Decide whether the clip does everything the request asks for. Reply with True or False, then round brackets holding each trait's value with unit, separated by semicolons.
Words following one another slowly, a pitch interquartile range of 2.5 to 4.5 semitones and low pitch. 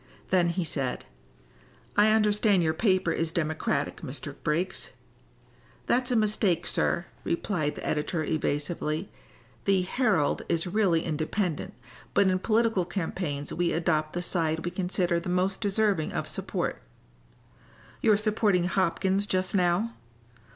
False (130 wpm; 3.8 semitones; 180 Hz)